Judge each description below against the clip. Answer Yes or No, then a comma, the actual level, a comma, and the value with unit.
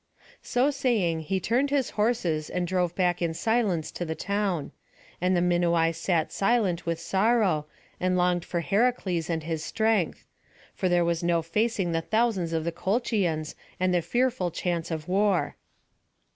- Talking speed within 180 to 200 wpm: No, average, 160 wpm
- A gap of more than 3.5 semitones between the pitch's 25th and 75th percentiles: Yes, average, 4.1 semitones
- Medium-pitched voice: Yes, medium, 180 Hz